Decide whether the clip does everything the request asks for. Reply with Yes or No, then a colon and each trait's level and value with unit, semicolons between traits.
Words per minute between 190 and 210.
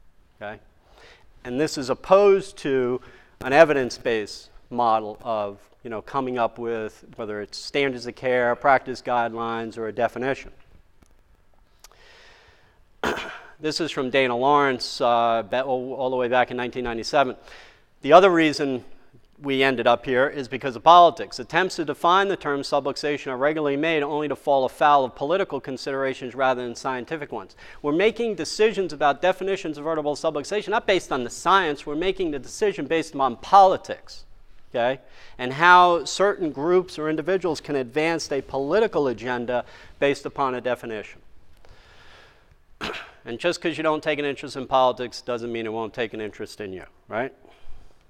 No: average, 155 wpm